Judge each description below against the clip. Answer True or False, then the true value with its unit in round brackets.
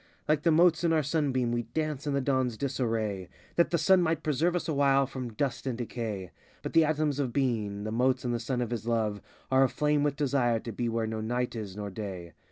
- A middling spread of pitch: True (4.5 semitones)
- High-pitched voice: False (130 Hz)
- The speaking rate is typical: False (235 wpm)